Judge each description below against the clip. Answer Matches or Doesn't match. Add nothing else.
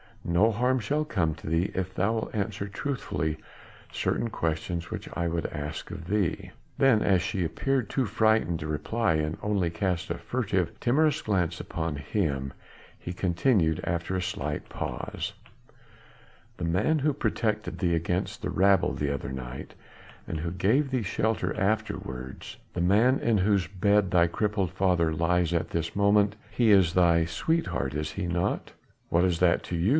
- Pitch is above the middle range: Doesn't match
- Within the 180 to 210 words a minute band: Doesn't match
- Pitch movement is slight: Doesn't match